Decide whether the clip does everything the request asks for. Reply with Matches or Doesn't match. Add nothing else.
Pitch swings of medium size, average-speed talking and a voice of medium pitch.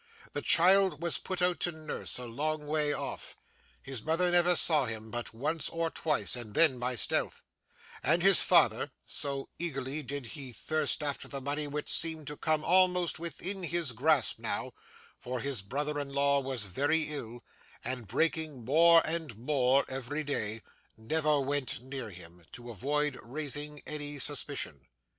Matches